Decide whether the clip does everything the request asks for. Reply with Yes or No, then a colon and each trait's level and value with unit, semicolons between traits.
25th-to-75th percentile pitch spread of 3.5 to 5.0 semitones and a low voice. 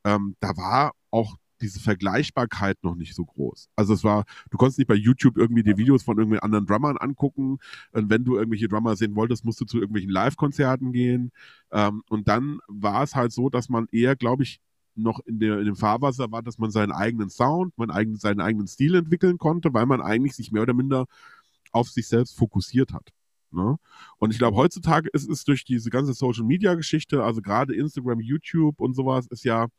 Yes: average, 3.8 semitones; low, 120 Hz